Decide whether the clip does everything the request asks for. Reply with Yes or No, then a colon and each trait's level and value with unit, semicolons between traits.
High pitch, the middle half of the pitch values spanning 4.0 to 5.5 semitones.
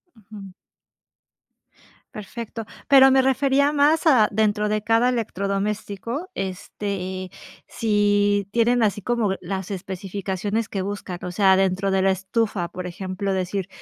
No: high, 205 Hz; average, 3.1 semitones